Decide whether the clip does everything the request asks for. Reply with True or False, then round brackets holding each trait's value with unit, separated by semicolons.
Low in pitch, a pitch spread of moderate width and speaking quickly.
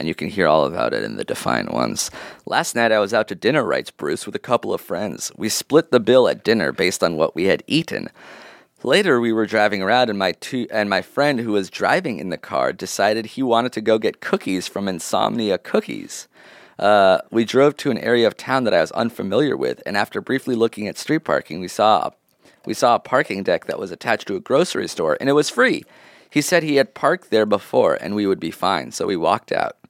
True (115 Hz; 4.6 semitones; 235 wpm)